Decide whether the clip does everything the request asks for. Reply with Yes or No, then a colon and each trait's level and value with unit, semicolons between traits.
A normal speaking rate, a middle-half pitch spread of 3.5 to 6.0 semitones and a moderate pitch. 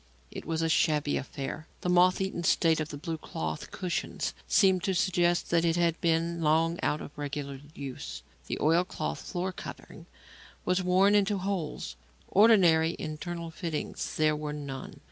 No: average, 165 wpm; average, 2.9 semitones; medium, 165 Hz